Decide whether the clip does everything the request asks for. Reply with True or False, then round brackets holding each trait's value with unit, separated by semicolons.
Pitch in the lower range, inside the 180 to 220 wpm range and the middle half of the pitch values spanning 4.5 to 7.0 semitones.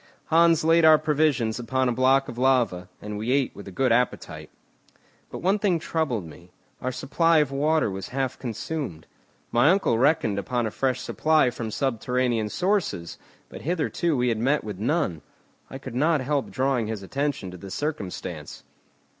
False (130 Hz; 170 wpm; 5.6 semitones)